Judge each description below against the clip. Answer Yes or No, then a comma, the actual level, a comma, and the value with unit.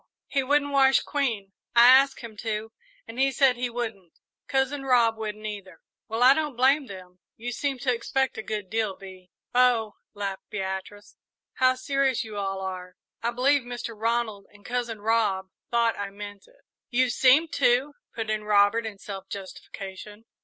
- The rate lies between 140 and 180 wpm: Yes, average, 170 wpm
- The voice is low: No, high, 230 Hz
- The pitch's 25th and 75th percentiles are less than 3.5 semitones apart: No, average, 4.1 semitones